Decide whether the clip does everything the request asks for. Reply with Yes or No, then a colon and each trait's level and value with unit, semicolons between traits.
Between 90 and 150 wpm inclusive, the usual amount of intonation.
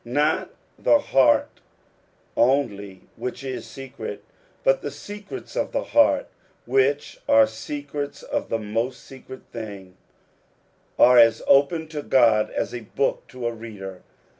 Yes: average, 140 wpm; average, 4.2 semitones